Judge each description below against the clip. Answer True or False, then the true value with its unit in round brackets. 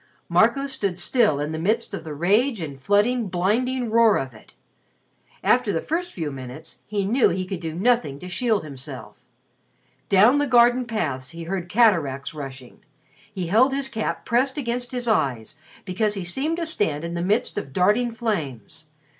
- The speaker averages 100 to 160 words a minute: False (175 wpm)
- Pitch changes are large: True (7.1 semitones)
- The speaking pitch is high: True (200 Hz)